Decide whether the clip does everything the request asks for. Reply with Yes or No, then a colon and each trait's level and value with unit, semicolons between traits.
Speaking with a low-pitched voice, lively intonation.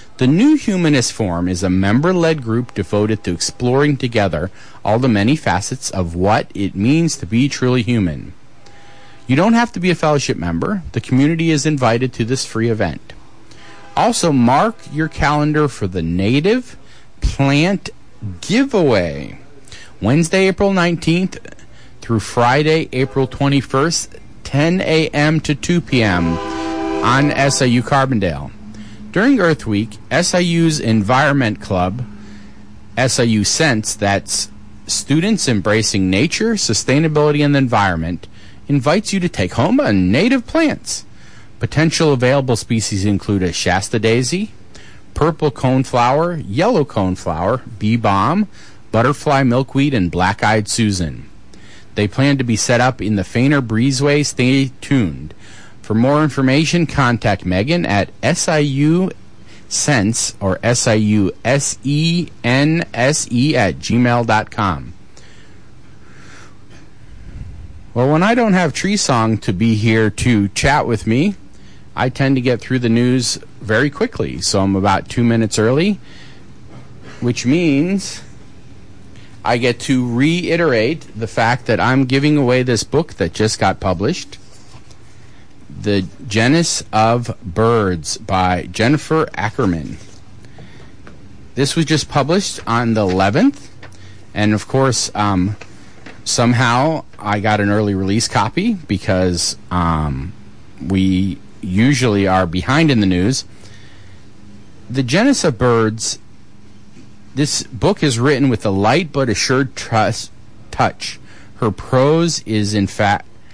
Yes: low, 120 Hz; wide, 5.9 semitones